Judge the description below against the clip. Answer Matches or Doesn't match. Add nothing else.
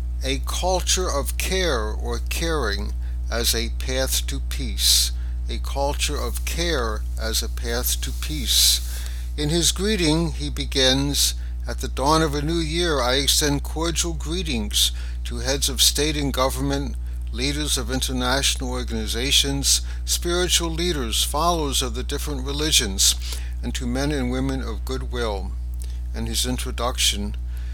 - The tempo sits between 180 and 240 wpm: Doesn't match